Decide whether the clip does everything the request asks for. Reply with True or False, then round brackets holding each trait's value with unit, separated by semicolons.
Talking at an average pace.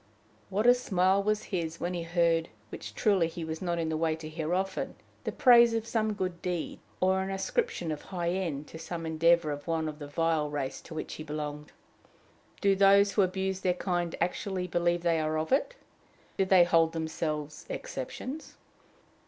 True (190 wpm)